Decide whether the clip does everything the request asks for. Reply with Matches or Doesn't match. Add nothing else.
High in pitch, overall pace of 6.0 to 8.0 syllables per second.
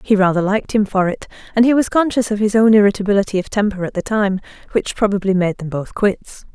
Matches